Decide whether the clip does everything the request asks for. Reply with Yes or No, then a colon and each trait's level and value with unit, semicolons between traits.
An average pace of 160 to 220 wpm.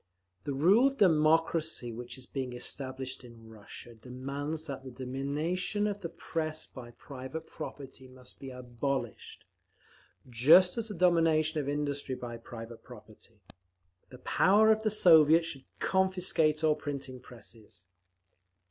No: average, 140 wpm